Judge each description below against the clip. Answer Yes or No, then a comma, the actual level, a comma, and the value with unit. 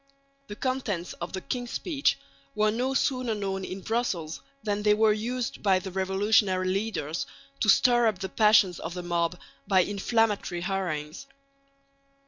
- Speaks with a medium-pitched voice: No, high, 205 Hz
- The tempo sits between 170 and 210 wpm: No, average, 150 wpm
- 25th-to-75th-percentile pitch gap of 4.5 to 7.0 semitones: No, average, 3.3 semitones